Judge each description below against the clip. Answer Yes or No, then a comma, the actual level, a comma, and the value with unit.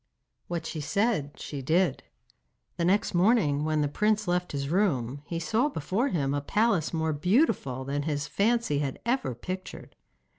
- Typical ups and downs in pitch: No, wide, 6.3 semitones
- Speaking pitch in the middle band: Yes, medium, 165 Hz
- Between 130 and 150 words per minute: No, average, 160 wpm